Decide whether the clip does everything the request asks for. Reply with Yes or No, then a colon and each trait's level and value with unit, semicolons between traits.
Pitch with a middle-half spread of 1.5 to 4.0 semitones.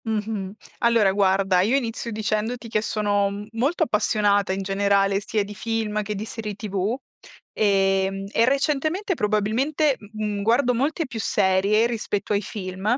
Yes: narrow, 2.6 semitones